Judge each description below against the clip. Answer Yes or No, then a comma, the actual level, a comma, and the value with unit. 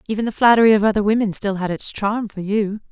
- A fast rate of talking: Yes, fast, 245 wpm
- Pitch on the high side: Yes, high, 210 Hz